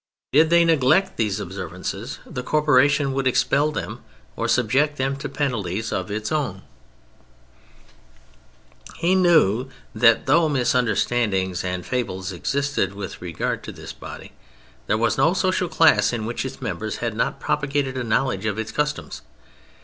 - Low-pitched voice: Yes, low, 125 Hz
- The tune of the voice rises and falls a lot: Yes, wide, 6.1 semitones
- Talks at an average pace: Yes, average, 145 wpm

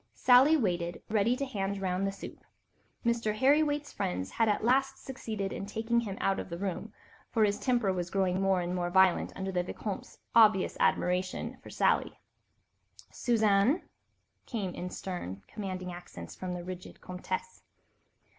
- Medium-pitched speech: No, high, 195 Hz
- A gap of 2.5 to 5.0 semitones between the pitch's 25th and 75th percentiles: Yes, average, 4.3 semitones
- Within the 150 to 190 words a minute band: Yes, average, 160 wpm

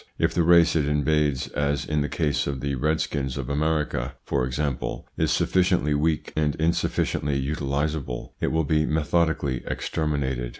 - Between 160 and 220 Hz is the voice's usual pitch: No, very low, 75 Hz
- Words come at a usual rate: Yes, average, 155 wpm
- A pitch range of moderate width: No, narrow, 2.2 semitones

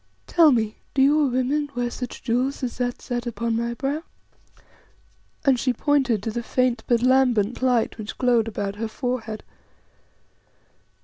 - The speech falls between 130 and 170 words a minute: Yes, average, 150 wpm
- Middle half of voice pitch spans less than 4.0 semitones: Yes, narrow, 2.4 semitones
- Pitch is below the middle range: No, high, 245 Hz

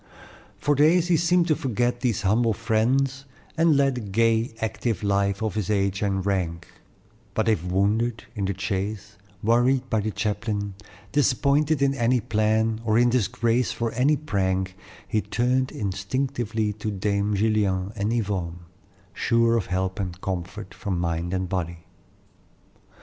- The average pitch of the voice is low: Yes, low, 110 Hz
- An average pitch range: Yes, average, 3.8 semitones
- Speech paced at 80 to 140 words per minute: No, average, 150 wpm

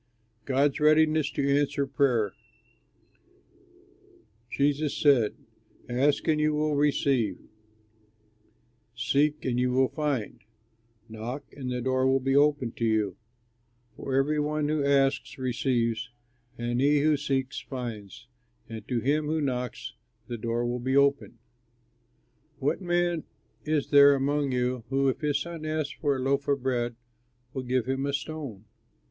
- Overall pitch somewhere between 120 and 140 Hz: Yes, low, 135 Hz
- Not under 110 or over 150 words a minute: Yes, average, 145 wpm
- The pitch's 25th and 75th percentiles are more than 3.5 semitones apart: No, average, 2.9 semitones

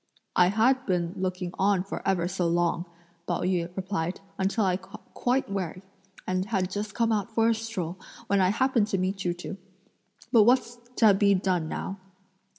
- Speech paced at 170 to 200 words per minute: Yes, average, 180 wpm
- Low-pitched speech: No, high, 195 Hz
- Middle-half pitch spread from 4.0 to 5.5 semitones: No, average, 3.1 semitones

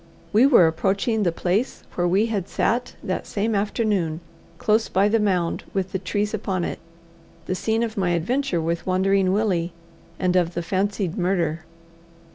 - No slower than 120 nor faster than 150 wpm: No, average, 165 wpm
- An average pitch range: Yes, average, 3.2 semitones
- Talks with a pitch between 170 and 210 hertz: Yes, high, 190 Hz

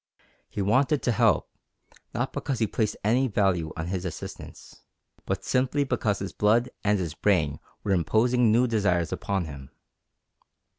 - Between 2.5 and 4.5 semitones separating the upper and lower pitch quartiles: No, average, 5.2 semitones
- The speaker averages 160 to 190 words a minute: No, average, 150 wpm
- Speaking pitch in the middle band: No, low, 105 Hz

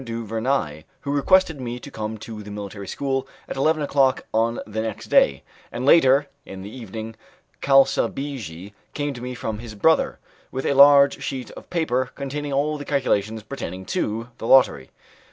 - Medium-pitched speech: No, low, 125 Hz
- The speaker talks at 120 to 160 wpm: No, average, 170 wpm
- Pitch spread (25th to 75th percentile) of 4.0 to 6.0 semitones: Yes, average, 4.3 semitones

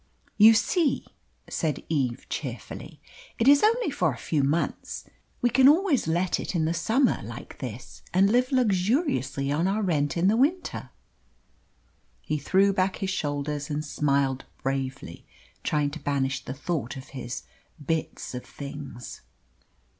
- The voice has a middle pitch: Yes, medium, 160 Hz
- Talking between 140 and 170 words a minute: Yes, average, 145 wpm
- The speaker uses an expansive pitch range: Yes, wide, 7.5 semitones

